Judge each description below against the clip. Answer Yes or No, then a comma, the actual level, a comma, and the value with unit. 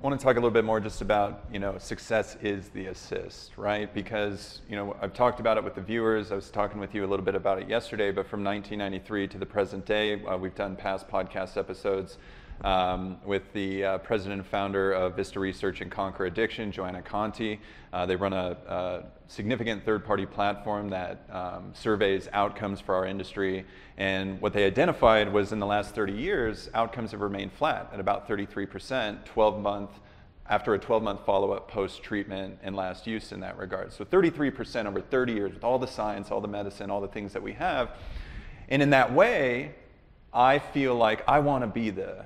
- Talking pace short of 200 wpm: No, fast, 205 wpm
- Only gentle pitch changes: Yes, narrow, 2.1 semitones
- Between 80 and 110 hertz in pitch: Yes, low, 100 Hz